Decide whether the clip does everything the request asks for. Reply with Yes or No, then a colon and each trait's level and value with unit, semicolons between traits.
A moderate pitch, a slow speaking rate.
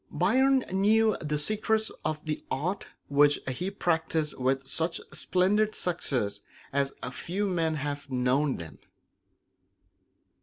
Yes: medium, 160 Hz; slow, 115 wpm